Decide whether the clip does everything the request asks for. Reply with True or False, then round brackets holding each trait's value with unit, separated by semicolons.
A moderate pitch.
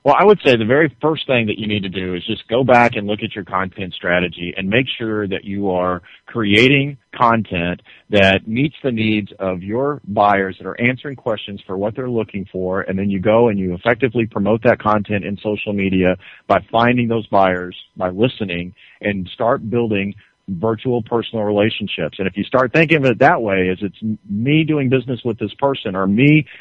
False (105 Hz)